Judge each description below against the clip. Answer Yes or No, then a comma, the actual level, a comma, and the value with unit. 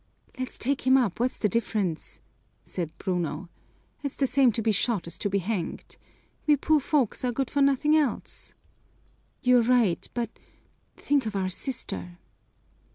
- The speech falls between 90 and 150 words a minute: No, average, 160 wpm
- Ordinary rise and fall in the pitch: No, wide, 5.8 semitones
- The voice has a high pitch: Yes, high, 235 Hz